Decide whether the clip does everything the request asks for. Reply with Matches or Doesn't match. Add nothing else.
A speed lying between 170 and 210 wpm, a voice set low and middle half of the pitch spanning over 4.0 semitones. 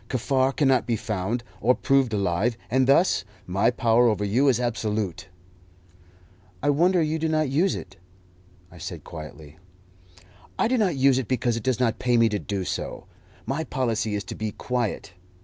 Matches